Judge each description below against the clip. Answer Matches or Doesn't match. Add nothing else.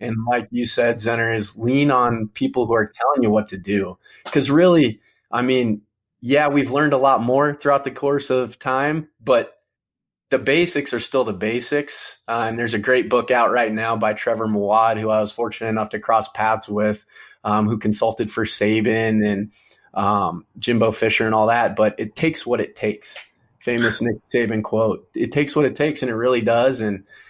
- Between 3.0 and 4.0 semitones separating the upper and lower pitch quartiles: Matches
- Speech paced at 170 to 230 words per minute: Matches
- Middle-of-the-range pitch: Doesn't match